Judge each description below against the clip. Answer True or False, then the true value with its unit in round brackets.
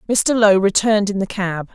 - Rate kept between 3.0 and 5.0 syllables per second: False (5.8 syllables/s)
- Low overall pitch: False (200 Hz)